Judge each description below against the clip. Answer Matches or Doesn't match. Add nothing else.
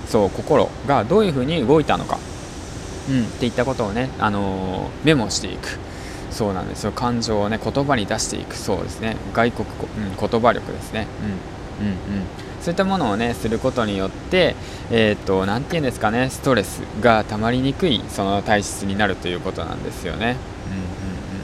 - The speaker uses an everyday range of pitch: Matches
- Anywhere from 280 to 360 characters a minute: Doesn't match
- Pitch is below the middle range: Matches